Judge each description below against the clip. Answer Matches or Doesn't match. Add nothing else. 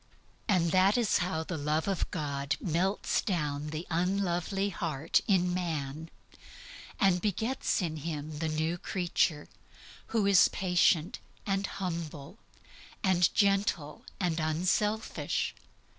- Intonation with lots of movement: Doesn't match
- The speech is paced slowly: Matches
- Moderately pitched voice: Matches